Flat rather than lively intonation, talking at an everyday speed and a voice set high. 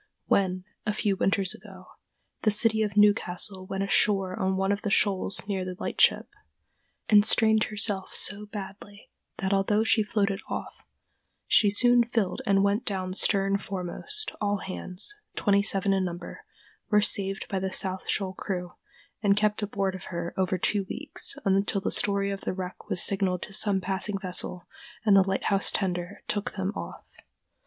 Yes: narrow, 1.6 semitones; average, 165 wpm; high, 195 Hz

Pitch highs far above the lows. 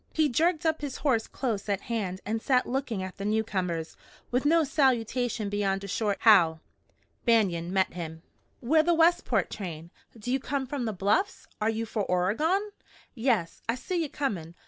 Yes: wide, 6.1 semitones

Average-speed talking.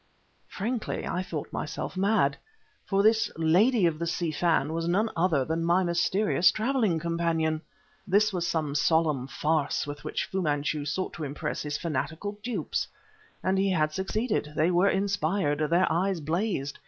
Yes: average, 160 wpm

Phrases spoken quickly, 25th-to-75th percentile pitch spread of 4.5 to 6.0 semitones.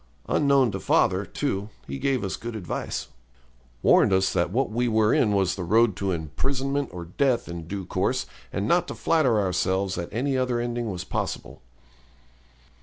No: average, 175 wpm; average, 5.2 semitones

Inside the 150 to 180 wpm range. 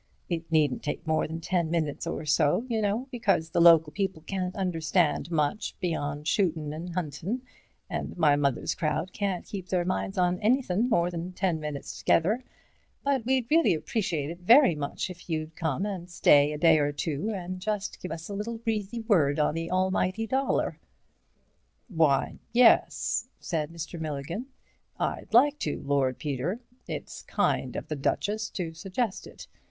Yes: average, 165 wpm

